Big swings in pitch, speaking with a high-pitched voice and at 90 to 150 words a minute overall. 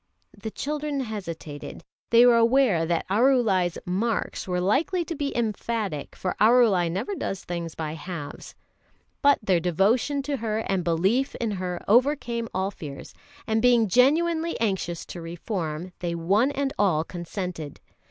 Yes: wide, 6.0 semitones; high, 205 Hz; average, 145 wpm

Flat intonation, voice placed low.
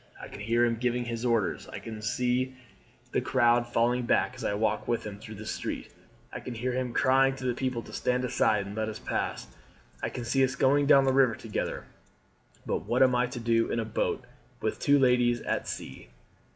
Yes: narrow, 1.9 semitones; low, 120 Hz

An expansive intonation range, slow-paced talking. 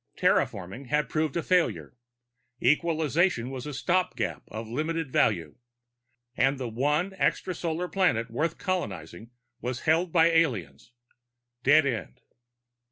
Yes: wide, 6.2 semitones; slow, 115 wpm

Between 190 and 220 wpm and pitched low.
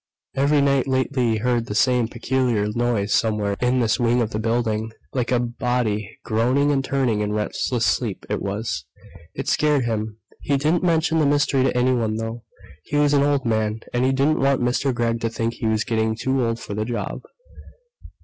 Yes: average, 195 wpm; low, 120 Hz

